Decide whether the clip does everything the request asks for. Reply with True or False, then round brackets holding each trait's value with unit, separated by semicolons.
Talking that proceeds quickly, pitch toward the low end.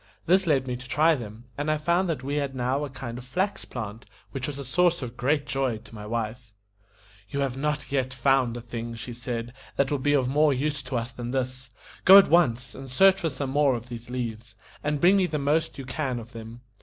True (240 wpm; 130 Hz)